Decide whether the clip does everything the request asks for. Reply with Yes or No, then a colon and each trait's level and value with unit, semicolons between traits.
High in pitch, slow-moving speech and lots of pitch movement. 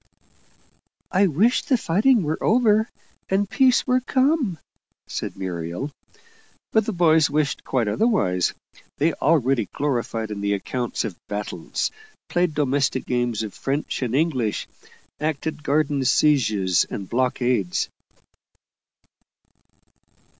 No: medium, 145 Hz; slow, 110 wpm; wide, 8.3 semitones